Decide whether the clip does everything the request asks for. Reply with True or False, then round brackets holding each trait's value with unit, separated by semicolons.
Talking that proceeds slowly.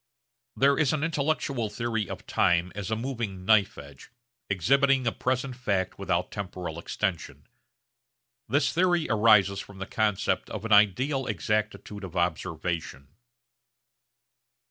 True (125 wpm)